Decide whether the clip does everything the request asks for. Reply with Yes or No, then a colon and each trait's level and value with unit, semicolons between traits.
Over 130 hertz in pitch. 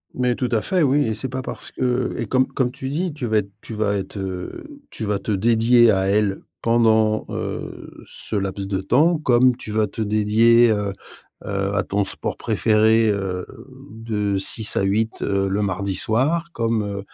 No: low, 110 Hz